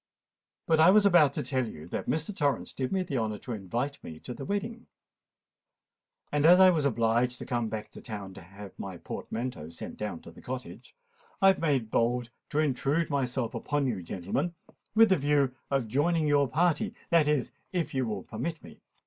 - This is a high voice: No, low, 135 Hz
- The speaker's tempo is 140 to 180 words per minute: No, average, 195 wpm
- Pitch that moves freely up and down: Yes, wide, 6.1 semitones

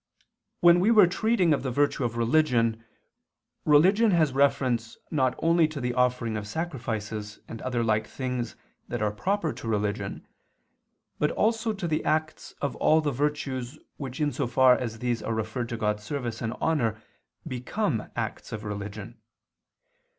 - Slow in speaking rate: No, average, 165 wpm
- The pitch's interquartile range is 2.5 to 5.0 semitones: No, wide, 5.5 semitones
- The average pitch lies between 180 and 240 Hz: No, low, 125 Hz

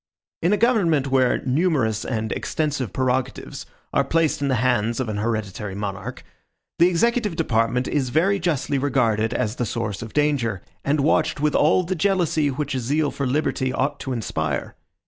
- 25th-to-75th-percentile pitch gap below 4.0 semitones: No, average, 5.3 semitones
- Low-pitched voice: Yes, low, 130 Hz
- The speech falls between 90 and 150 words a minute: No, average, 170 wpm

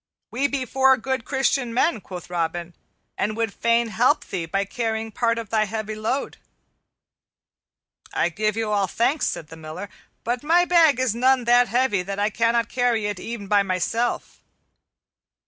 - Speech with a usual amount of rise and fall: Yes, average, 3.7 semitones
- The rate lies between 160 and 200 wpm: Yes, average, 165 wpm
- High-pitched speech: Yes, high, 225 Hz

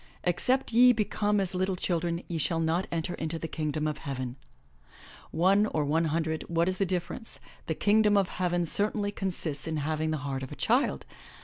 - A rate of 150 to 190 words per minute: No, average, 200 wpm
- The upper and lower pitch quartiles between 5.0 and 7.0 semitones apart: No, average, 3.6 semitones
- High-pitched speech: No, medium, 170 Hz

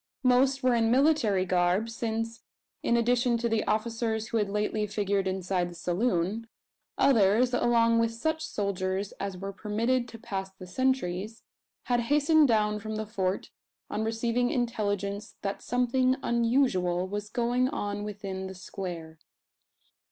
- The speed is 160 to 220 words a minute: No, average, 145 wpm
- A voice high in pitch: Yes, high, 220 Hz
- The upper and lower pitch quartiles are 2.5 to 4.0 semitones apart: Yes, average, 3.5 semitones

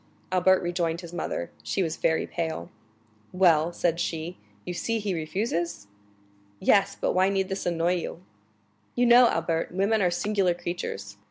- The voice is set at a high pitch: No, medium, 175 Hz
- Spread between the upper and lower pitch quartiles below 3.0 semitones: Yes, narrow, 2.6 semitones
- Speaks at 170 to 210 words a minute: No, average, 155 wpm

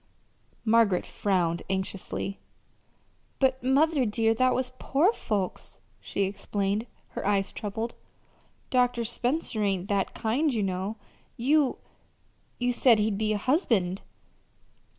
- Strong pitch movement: No, average, 4.3 semitones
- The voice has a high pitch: Yes, high, 220 Hz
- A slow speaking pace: Yes, slow, 115 wpm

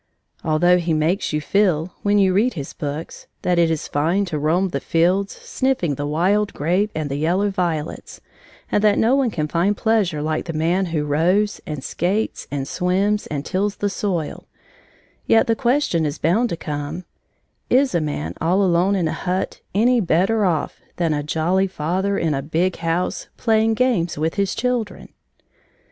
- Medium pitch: Yes, medium, 180 Hz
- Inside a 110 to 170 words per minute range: No, average, 180 wpm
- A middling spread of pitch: Yes, average, 4.5 semitones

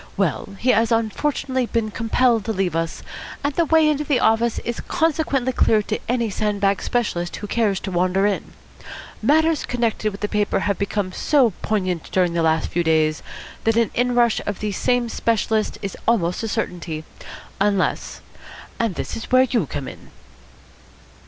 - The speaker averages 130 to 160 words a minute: No, average, 170 wpm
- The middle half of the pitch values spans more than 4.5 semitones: No, average, 4.0 semitones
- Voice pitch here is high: Yes, high, 220 Hz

